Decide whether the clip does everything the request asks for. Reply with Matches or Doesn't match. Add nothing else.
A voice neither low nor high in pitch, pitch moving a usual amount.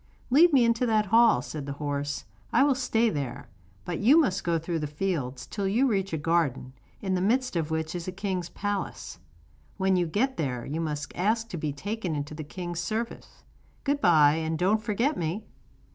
Doesn't match